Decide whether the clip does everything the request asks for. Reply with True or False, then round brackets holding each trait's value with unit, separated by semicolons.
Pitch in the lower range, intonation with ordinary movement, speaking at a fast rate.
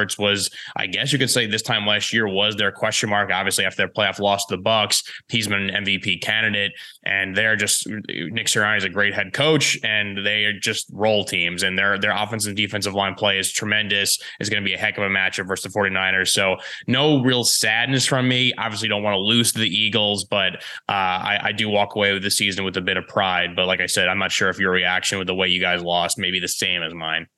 False (100 Hz; 1.9 semitones; 255 wpm)